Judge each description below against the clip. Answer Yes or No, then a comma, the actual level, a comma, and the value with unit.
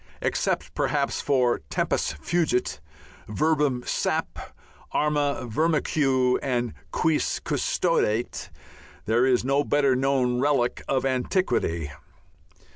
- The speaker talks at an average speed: No, slow, 95 wpm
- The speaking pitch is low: Yes, low, 130 Hz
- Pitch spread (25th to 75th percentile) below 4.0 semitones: Yes, average, 3.0 semitones